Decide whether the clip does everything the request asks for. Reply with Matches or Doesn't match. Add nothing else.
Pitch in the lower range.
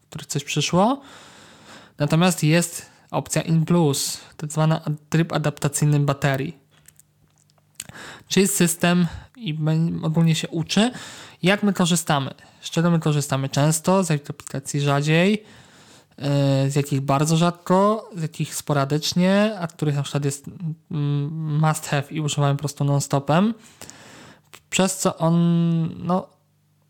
Doesn't match